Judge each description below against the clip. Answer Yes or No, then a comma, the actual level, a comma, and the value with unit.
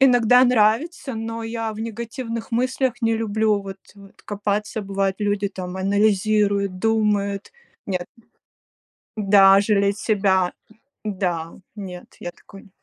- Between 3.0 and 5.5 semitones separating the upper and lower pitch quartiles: No, narrow, 2.4 semitones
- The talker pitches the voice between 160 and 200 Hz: No, high, 210 Hz